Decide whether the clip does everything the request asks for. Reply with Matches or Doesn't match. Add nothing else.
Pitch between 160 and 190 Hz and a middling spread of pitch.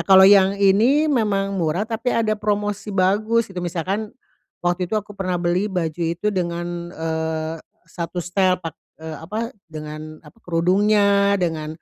Matches